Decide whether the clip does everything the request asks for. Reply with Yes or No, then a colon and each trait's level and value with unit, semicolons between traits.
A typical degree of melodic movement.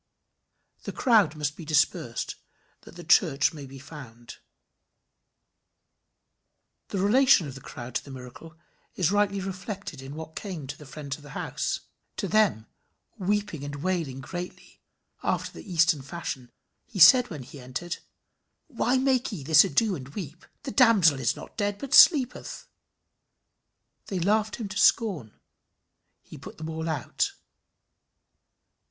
No: wide, 6.4 semitones